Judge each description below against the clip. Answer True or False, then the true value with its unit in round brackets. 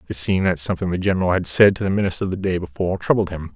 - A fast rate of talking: True (270 wpm)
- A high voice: False (90 Hz)